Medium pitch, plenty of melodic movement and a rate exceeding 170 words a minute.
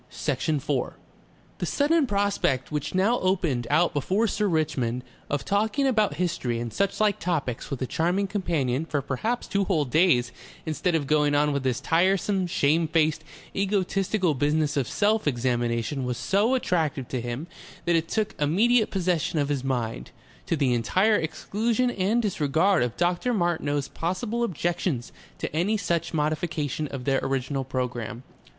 No: medium, 160 Hz; wide, 6.2 semitones; average, 155 wpm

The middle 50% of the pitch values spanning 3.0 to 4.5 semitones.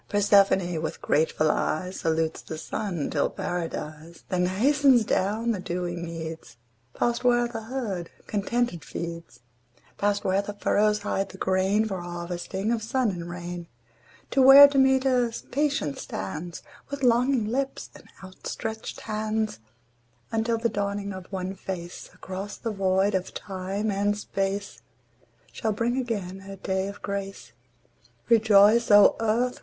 Yes: average, 4.0 semitones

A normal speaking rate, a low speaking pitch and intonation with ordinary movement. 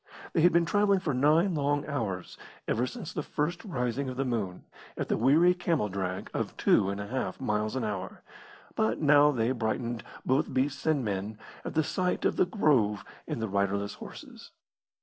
No: average, 190 wpm; low, 130 Hz; wide, 6.6 semitones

